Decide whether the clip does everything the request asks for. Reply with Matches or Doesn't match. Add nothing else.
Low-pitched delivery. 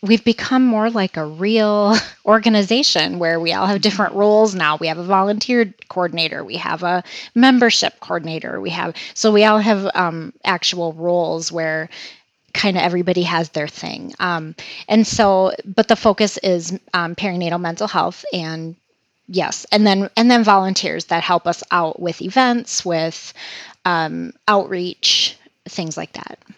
Doesn't match